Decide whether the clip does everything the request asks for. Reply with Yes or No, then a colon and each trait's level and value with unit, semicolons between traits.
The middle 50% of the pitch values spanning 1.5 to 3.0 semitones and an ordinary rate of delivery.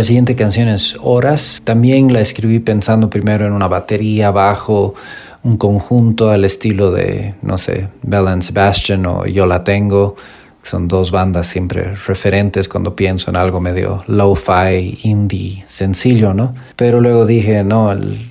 Yes: narrow, 2.6 semitones; average, 155 wpm